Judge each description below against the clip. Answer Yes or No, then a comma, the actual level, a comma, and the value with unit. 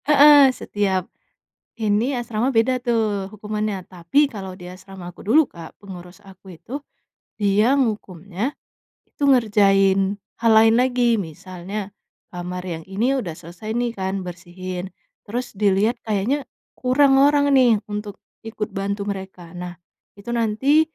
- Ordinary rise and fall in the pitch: Yes, average, 4.2 semitones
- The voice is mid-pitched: No, high, 205 Hz